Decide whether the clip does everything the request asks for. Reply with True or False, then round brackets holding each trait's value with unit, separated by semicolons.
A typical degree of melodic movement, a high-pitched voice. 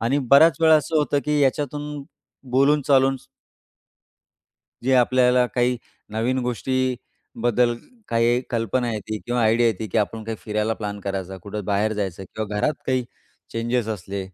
False (3.4 semitones; 120 Hz)